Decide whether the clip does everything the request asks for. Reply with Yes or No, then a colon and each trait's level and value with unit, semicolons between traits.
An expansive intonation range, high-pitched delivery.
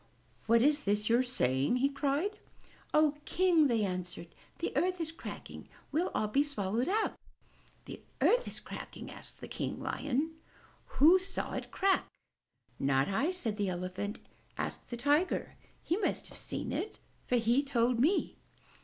Yes: wide, 7.4 semitones; very high, 275 Hz